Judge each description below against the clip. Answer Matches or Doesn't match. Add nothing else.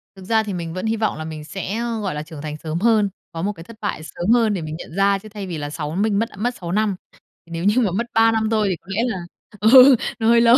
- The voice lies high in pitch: Matches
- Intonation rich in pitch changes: Doesn't match